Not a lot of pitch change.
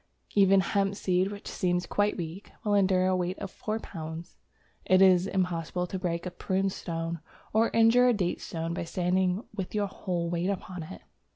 Yes: narrow, 2.2 semitones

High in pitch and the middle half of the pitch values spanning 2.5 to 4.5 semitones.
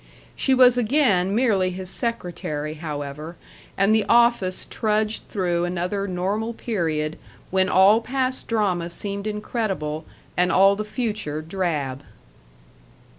Yes: high, 195 Hz; average, 4.2 semitones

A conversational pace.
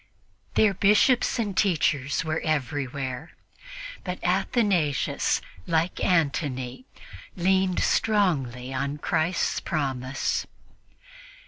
No: slow, 80 wpm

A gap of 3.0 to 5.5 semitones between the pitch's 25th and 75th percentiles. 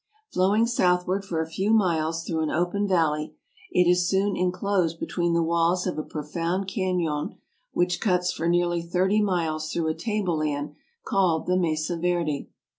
No: narrow, 2.4 semitones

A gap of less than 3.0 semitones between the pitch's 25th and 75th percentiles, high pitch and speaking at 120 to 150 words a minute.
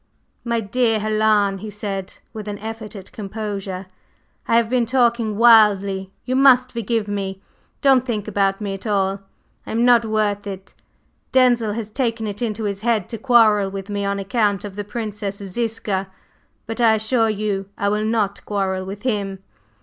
No: narrow, 2.5 semitones; high, 210 Hz; average, 175 wpm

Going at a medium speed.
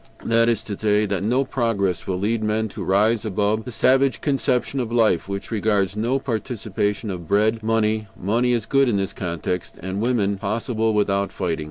Yes: average, 185 wpm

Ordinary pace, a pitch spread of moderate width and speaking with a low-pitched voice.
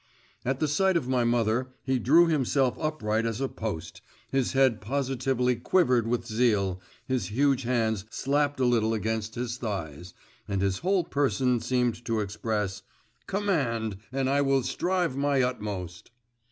Yes: average, 155 wpm; average, 3.7 semitones; low, 125 Hz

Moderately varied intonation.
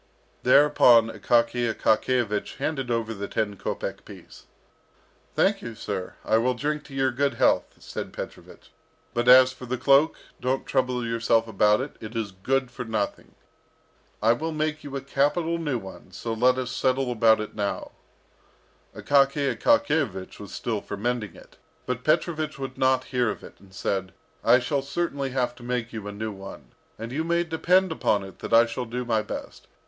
Yes: average, 3.7 semitones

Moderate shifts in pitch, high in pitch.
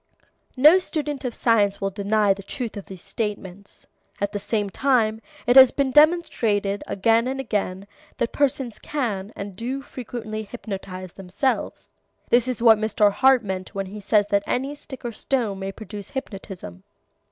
Yes: average, 4.2 semitones; high, 215 Hz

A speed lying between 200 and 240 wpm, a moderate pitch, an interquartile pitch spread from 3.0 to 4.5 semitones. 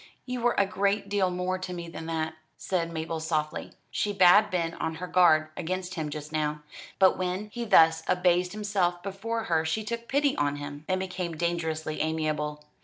No: average, 185 wpm; medium, 175 Hz; average, 3.4 semitones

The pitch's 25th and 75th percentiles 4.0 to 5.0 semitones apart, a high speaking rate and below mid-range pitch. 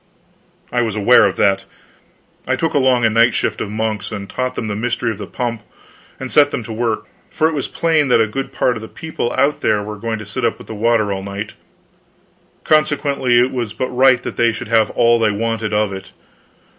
No: average, 3.1 semitones; fast, 225 wpm; low, 115 Hz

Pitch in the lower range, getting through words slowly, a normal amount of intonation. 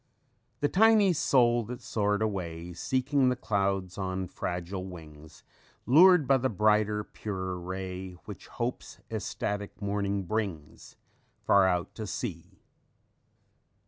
Yes: low, 100 Hz; slow, 120 wpm; average, 4.5 semitones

